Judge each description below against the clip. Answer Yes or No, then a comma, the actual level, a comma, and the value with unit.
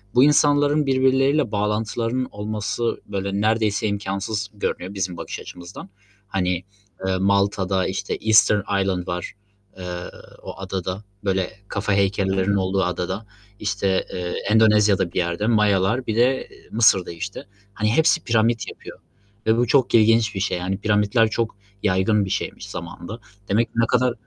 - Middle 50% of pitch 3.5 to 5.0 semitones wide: No, average, 3.0 semitones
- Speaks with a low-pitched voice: Yes, low, 105 Hz